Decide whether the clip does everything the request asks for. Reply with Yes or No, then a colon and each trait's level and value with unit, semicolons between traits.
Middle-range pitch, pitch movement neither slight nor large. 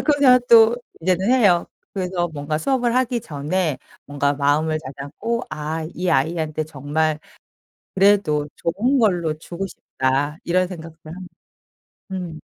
Yes: medium, 170 Hz; average, 4.6 semitones